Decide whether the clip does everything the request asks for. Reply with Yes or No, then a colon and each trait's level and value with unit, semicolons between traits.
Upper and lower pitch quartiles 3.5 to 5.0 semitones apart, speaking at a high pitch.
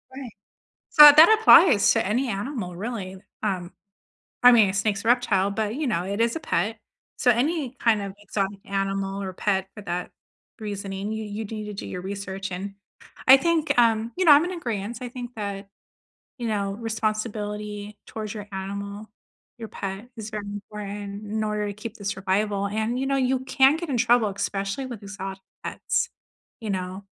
No: average, 3.1 semitones; high, 210 Hz